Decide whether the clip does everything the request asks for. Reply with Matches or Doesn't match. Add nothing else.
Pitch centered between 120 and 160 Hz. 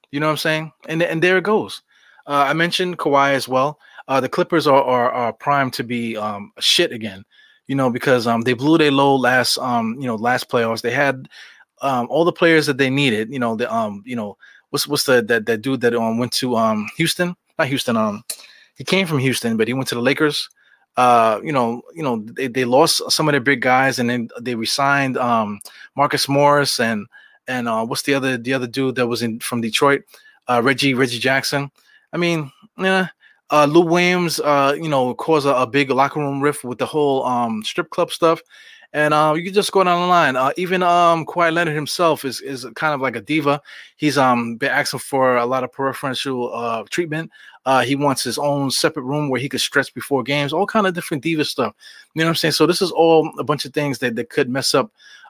Matches